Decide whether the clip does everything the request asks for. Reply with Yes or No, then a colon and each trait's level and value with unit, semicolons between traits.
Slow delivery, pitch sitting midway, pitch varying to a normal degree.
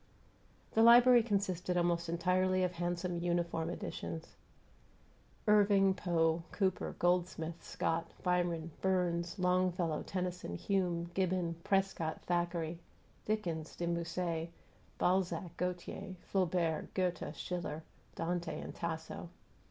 No: slow, 100 wpm; medium, 175 Hz; narrow, 1.7 semitones